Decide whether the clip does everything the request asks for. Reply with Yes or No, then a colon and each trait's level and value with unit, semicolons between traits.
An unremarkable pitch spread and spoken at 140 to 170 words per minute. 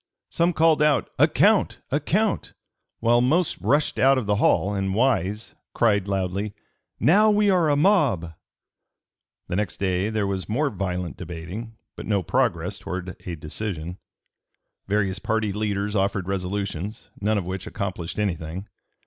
Yes: average, 4.3 semitones; average, 150 wpm